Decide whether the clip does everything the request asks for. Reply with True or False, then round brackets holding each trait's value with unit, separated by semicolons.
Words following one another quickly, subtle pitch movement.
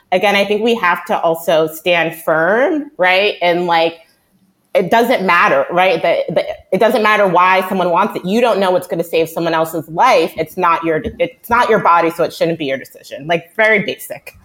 False (210 wpm; 3.8 semitones)